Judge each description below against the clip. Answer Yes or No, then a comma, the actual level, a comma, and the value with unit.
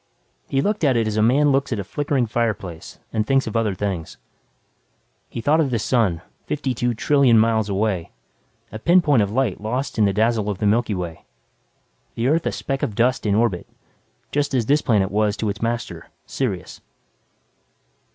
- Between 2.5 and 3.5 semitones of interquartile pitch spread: No, average, 4.5 semitones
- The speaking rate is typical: Yes, average, 180 wpm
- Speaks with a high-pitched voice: No, low, 115 Hz